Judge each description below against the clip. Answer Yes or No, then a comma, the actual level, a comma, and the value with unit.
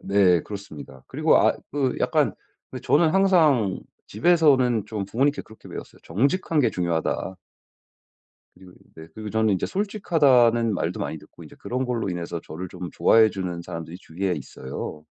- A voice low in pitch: Yes, low, 110 Hz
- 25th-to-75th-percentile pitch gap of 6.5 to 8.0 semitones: Yes, wide, 7.1 semitones